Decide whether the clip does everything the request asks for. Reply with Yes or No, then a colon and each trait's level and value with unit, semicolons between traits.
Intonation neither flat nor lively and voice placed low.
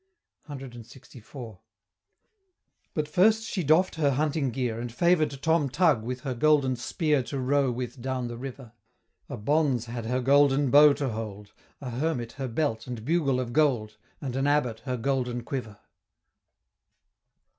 Yes: average, 3.5 semitones; low, 130 Hz